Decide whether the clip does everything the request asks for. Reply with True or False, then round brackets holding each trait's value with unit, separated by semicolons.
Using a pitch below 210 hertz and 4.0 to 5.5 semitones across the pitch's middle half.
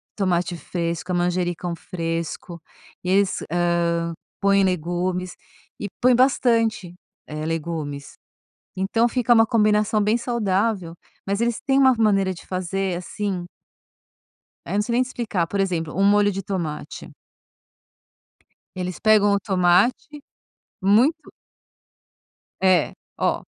False (190 Hz; 3.5 semitones)